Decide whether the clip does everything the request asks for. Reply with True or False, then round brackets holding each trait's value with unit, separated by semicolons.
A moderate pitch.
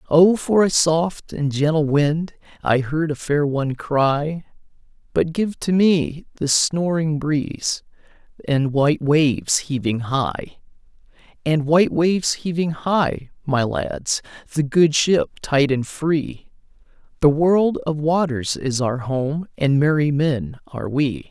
True (150 Hz)